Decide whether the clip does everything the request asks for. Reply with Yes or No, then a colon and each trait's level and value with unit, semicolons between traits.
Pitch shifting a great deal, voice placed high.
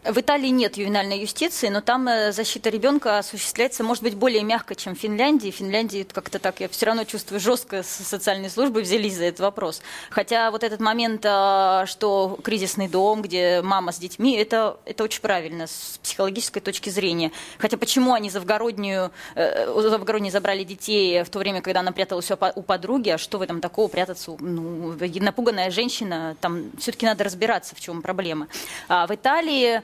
No: average, 3.2 semitones; high, 205 Hz